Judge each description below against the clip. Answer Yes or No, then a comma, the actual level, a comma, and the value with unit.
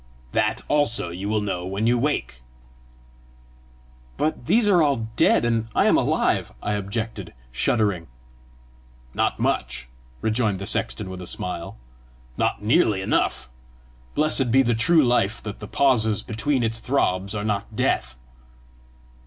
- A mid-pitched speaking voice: No, low, 110 Hz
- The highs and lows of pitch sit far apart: No, average, 4.4 semitones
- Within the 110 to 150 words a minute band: Yes, average, 145 wpm